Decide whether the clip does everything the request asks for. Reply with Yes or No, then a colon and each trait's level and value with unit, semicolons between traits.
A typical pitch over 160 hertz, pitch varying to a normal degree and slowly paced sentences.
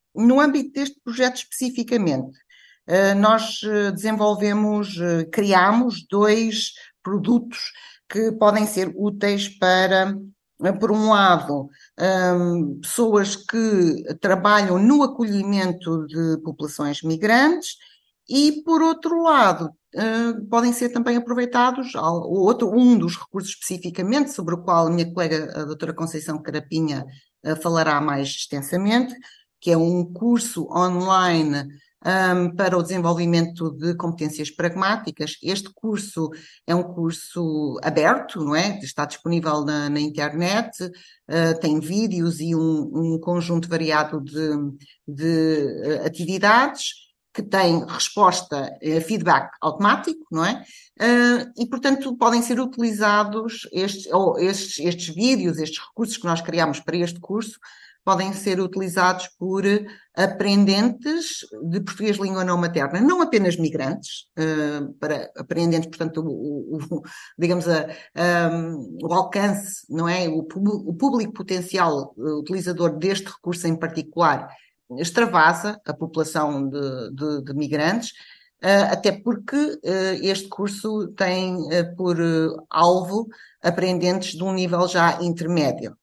Yes: medium, 185 Hz; average, 4.8 semitones; slow, 115 wpm